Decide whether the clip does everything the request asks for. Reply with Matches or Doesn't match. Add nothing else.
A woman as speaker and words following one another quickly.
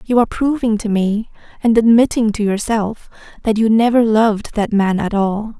Doesn't match